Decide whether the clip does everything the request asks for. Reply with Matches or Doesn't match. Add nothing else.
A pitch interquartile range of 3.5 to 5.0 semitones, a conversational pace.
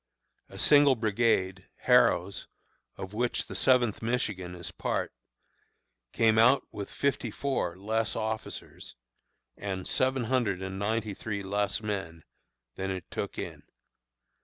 Doesn't match